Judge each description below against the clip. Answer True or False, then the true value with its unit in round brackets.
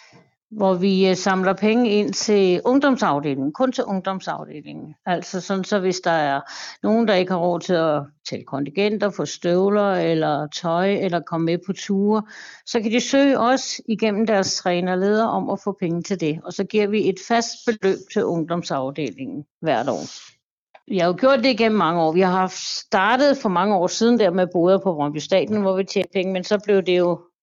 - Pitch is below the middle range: False (190 Hz)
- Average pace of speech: True (195 wpm)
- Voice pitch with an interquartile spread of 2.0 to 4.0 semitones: True (3.5 semitones)